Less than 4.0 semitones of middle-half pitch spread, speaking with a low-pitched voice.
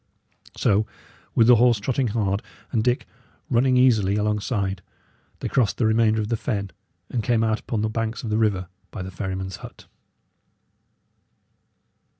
Yes: narrow, 2.6 semitones; low, 110 Hz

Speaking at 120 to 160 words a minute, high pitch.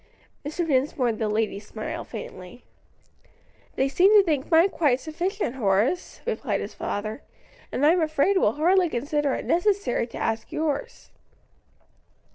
Yes: average, 140 wpm; very high, 285 Hz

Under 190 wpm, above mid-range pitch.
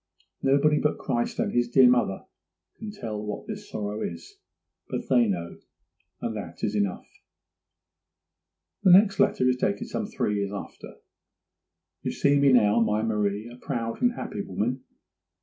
No: average, 155 wpm; low, 115 Hz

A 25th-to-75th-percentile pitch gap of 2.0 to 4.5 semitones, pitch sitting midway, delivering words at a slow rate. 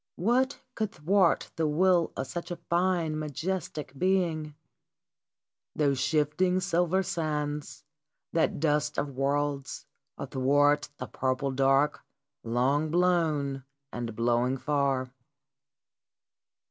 Yes: average, 4.0 semitones; medium, 150 Hz; slow, 100 wpm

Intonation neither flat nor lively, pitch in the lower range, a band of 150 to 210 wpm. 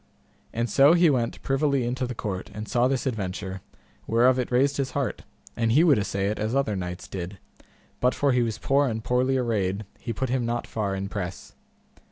Yes: average, 4.3 semitones; low, 120 Hz; fast, 205 wpm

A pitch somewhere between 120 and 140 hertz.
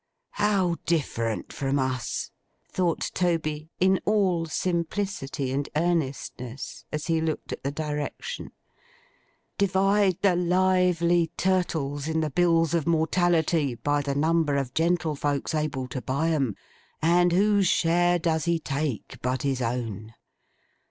No: medium, 160 Hz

